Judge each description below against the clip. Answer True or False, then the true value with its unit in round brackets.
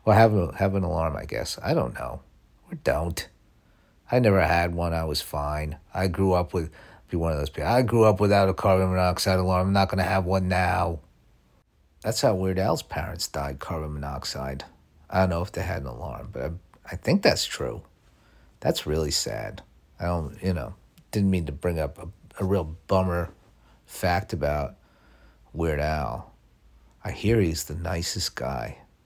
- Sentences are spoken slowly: False (190 wpm)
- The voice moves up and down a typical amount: True (3.8 semitones)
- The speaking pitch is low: True (90 Hz)